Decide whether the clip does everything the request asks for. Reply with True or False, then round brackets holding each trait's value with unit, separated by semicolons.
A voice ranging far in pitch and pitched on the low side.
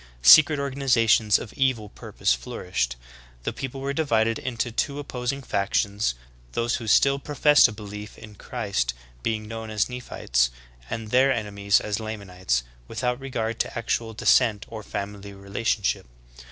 False (3.7 semitones; 110 Hz)